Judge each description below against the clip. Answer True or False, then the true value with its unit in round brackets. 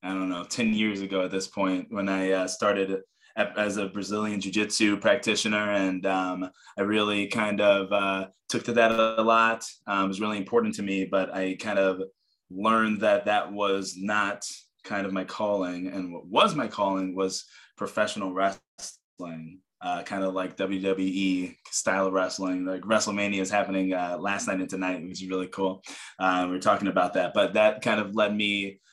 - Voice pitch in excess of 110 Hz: False (95 Hz)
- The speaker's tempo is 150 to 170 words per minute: False (190 wpm)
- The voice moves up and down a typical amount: False (1.7 semitones)